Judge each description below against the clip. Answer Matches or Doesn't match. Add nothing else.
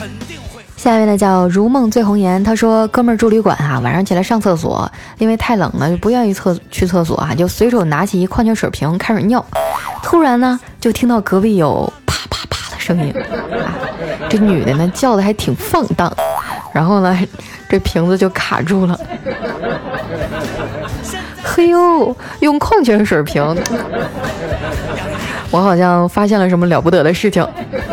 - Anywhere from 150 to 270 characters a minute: Matches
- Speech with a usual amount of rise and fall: Matches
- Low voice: Doesn't match